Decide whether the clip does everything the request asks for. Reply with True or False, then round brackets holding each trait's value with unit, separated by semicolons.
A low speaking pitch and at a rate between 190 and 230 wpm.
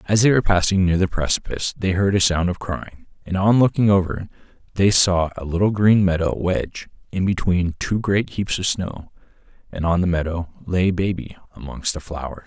True (90 Hz; 195 wpm)